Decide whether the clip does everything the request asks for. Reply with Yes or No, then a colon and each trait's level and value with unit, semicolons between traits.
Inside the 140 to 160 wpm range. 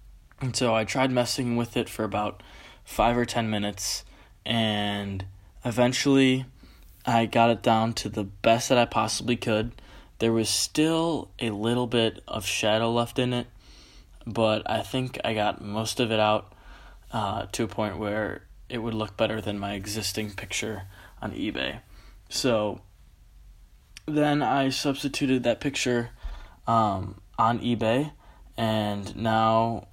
Yes: average, 145 wpm